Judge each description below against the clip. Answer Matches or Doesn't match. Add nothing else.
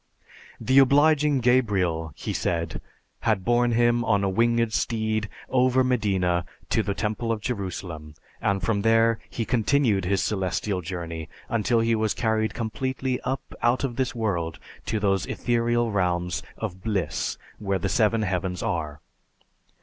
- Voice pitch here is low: Matches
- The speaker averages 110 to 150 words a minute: Matches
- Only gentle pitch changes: Doesn't match